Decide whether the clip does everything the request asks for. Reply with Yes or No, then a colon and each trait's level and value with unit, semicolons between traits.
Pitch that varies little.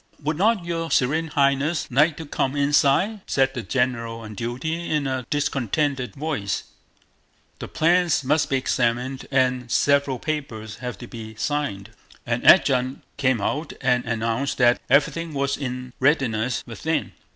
No: average, 3.5 semitones